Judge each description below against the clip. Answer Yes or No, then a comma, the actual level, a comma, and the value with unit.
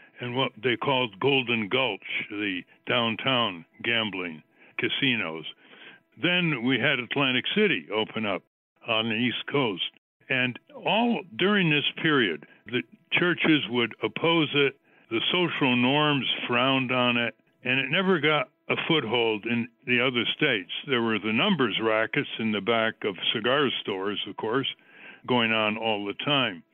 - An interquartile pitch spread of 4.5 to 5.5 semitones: Yes, average, 5.0 semitones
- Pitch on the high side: No, low, 125 Hz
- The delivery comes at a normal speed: Yes, average, 145 wpm